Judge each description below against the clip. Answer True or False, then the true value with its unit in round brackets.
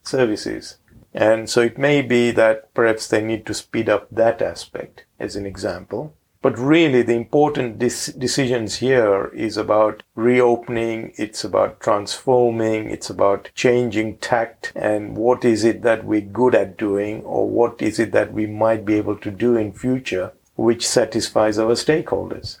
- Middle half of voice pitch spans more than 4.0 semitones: False (2.4 semitones)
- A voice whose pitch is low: True (115 Hz)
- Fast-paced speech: False (160 wpm)